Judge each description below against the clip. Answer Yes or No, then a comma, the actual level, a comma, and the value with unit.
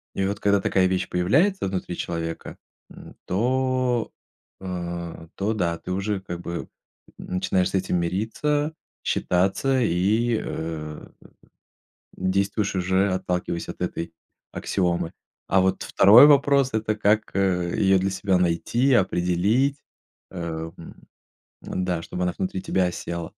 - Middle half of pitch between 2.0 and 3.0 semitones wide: No, average, 3.5 semitones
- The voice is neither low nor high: No, very low, 95 Hz